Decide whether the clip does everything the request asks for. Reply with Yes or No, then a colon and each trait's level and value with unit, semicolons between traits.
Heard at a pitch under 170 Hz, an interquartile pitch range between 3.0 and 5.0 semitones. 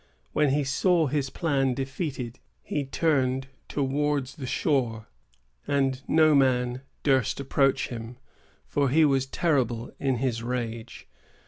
No: low, 135 Hz; narrow, 2.5 semitones